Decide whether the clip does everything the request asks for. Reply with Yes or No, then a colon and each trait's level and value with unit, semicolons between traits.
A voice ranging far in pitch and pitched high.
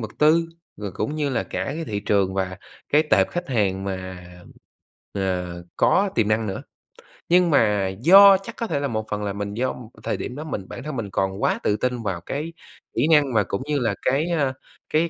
No: wide, 7.5 semitones; low, 115 Hz